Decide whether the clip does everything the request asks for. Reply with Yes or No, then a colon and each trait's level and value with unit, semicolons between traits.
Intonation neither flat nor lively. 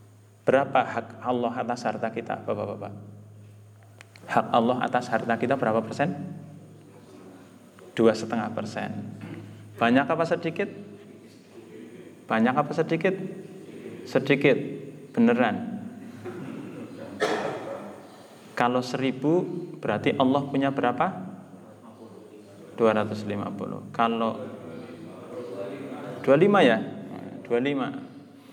No: wide, 6.9 semitones